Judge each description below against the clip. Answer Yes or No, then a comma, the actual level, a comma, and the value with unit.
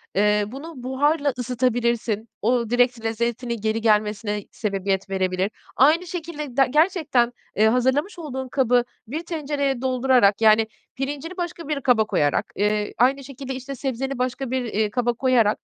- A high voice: Yes, very high, 250 Hz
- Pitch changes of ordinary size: Yes, average, 4.0 semitones